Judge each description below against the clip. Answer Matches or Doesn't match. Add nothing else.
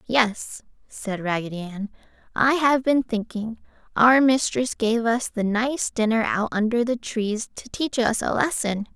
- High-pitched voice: Matches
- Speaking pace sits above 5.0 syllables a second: Doesn't match